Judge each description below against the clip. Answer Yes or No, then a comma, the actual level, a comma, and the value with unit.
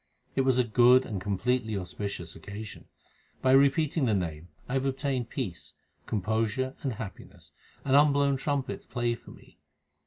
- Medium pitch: No, low, 125 Hz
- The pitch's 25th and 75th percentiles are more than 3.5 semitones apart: Yes, average, 4.5 semitones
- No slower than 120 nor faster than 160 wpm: Yes, average, 150 wpm